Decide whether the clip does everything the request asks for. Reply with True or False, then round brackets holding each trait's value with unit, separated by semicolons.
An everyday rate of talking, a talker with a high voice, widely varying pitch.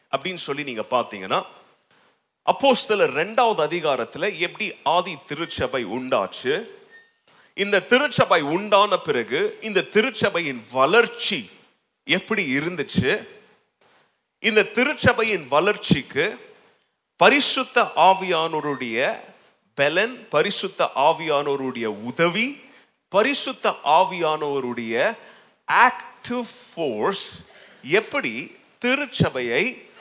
False (70 wpm; 205 Hz; 8.4 semitones)